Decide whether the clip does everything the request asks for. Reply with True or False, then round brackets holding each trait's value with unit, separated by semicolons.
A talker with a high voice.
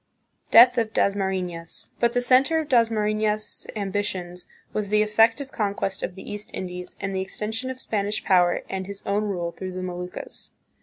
True (205 Hz)